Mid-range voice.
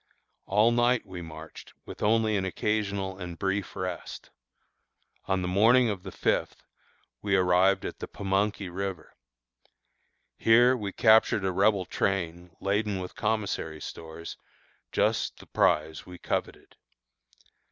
No: very low, 95 Hz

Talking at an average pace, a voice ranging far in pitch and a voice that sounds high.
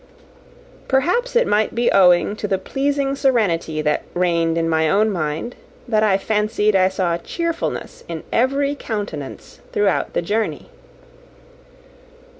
No: slow, 130 wpm; wide, 7.3 semitones; high, 210 Hz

